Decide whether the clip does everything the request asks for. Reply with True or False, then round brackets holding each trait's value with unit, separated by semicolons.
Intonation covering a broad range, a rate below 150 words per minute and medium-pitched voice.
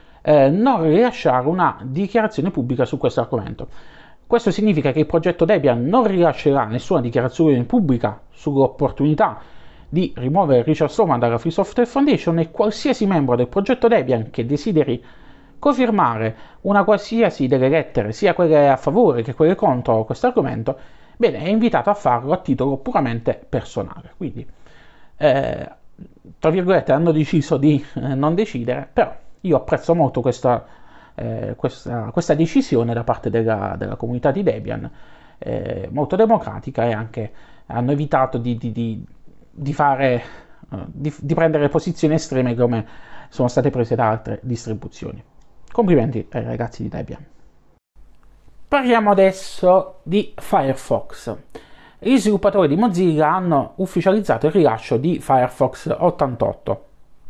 True (7.2 semitones; 135 wpm; 150 Hz)